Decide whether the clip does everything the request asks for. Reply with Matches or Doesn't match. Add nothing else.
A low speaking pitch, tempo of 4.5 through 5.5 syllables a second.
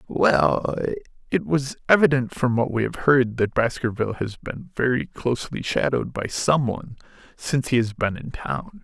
Matches